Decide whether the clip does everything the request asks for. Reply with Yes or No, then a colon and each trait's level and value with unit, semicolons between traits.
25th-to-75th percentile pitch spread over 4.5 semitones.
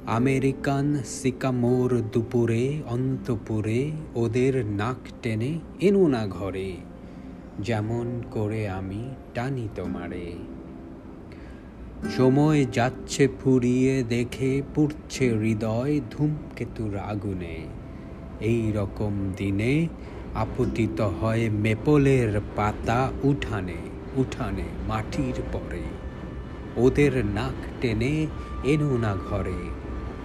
Yes: average, 5.2 semitones